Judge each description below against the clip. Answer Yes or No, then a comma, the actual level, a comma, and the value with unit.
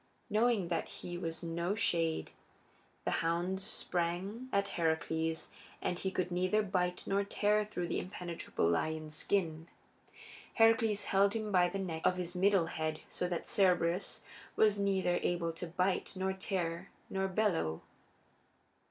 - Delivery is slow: No, average, 145 wpm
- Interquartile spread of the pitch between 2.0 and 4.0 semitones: Yes, average, 2.9 semitones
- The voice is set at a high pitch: No, medium, 180 Hz